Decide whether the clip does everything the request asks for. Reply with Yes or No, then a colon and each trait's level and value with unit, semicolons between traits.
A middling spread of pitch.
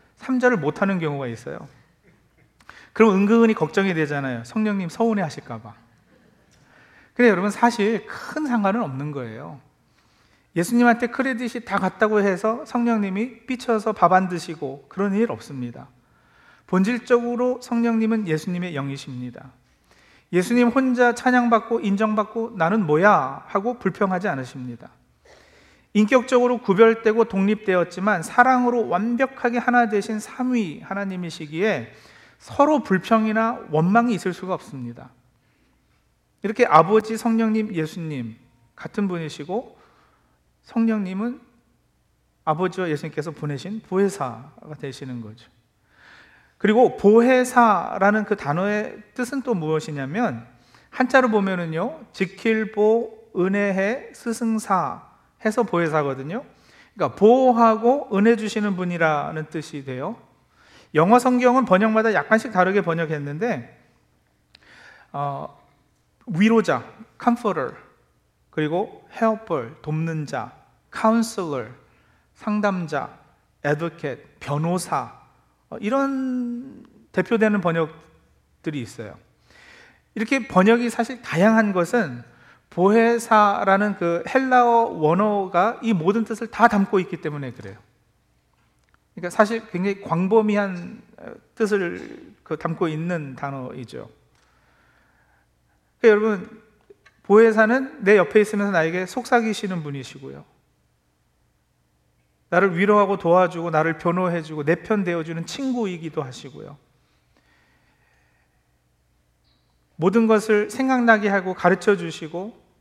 No: wide, 6.6 semitones